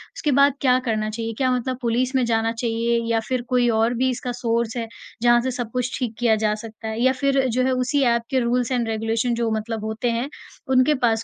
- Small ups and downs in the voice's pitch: Yes, narrow, 2.0 semitones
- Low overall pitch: No, high, 235 Hz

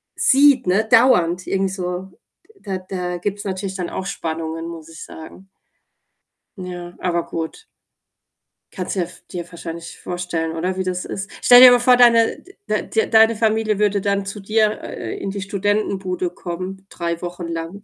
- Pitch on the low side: No, high, 190 Hz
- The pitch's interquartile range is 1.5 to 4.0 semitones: Yes, average, 3.1 semitones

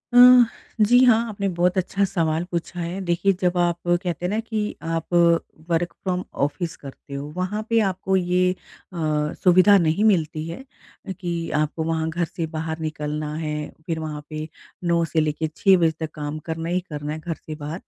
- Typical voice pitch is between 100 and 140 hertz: No, medium, 170 Hz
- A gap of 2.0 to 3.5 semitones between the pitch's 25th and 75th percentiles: Yes, average, 2.8 semitones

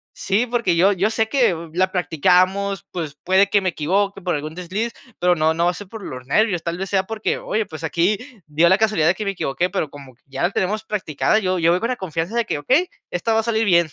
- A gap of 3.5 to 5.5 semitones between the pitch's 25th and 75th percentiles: Yes, average, 3.9 semitones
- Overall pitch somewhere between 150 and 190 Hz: Yes, medium, 185 Hz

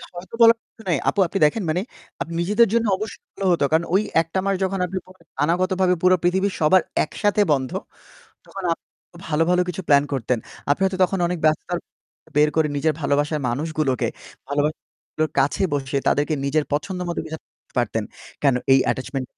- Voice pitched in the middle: Yes, medium, 165 Hz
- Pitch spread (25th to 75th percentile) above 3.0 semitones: Yes, average, 4.5 semitones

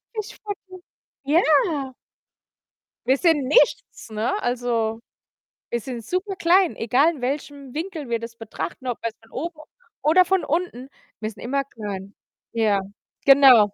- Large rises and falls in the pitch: Yes, wide, 6.1 semitones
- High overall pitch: Yes, very high, 265 Hz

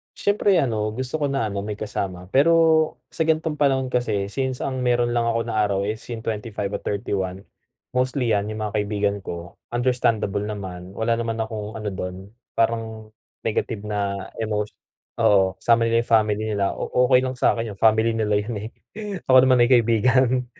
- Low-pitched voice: Yes, low, 110 Hz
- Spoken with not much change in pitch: No, average, 3.4 semitones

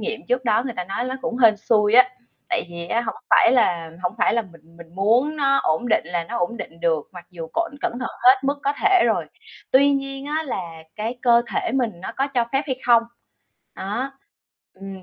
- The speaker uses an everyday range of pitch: No, wide, 6.6 semitones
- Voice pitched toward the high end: Yes, high, 230 Hz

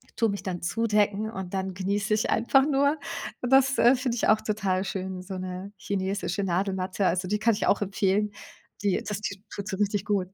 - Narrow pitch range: Yes, narrow, 2.3 semitones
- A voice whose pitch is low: No, high, 200 Hz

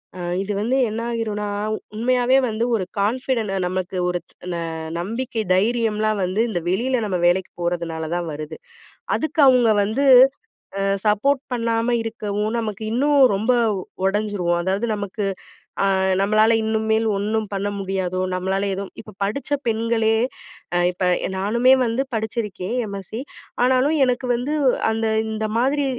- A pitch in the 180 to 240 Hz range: Yes, high, 215 Hz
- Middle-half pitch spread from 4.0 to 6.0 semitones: No, average, 3.3 semitones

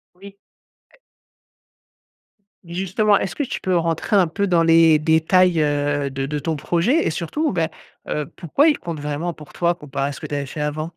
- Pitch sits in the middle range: Yes, medium, 165 Hz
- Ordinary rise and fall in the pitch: Yes, average, 3.7 semitones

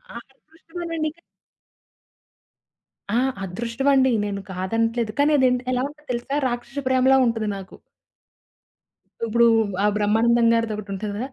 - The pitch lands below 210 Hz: No, high, 235 Hz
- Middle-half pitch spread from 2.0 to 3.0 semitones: No, average, 3.8 semitones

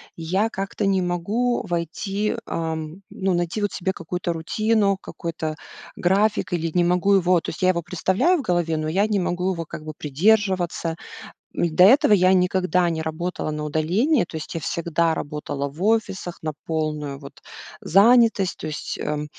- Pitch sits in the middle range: Yes, medium, 175 Hz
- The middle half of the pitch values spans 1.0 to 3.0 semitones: No, average, 3.5 semitones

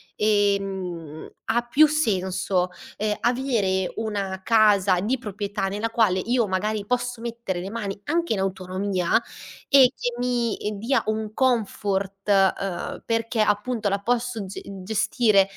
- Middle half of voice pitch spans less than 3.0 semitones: No, average, 3.3 semitones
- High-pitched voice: Yes, high, 210 Hz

